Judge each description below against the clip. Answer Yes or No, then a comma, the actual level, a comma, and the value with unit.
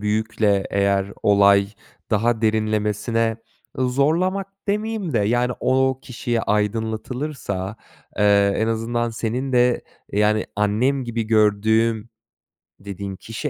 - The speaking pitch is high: No, low, 110 Hz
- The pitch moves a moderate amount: Yes, average, 3.0 semitones